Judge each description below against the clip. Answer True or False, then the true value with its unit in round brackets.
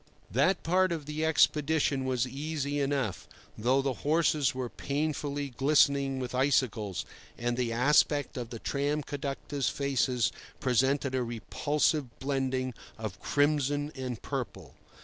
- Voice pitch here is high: False (140 Hz)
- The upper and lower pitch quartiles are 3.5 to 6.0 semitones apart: False (2.4 semitones)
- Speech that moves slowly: True (130 wpm)